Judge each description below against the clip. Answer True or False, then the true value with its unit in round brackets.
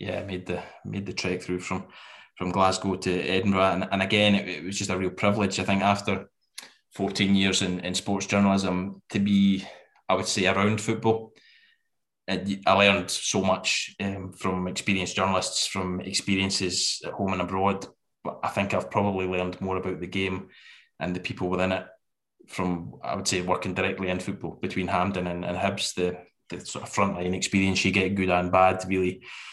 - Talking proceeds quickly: False (190 wpm)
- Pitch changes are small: True (1.3 semitones)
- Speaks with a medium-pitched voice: False (95 Hz)